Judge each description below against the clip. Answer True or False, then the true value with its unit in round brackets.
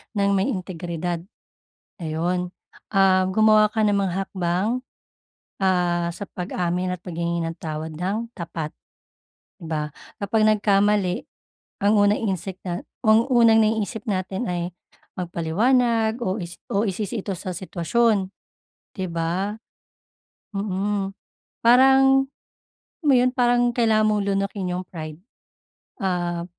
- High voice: True (195 Hz)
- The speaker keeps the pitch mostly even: False (3.7 semitones)